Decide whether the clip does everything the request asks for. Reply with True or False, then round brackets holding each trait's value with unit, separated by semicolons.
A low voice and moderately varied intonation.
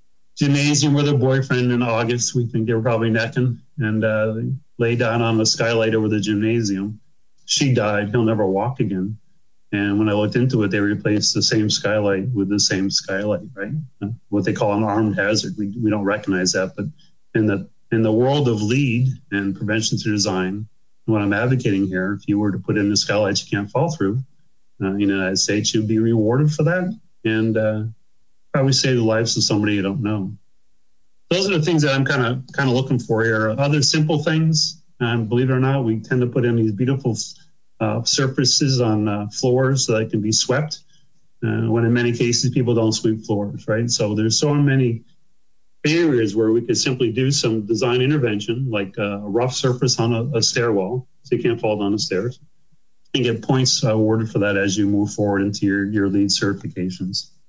True (115 Hz; 3.9 semitones)